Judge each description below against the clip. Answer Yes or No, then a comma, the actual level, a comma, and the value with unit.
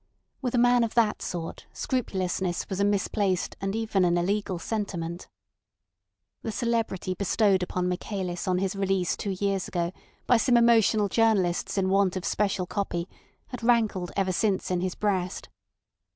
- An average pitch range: Yes, average, 3.1 semitones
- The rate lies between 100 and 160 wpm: Yes, average, 155 wpm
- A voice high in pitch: Yes, high, 195 Hz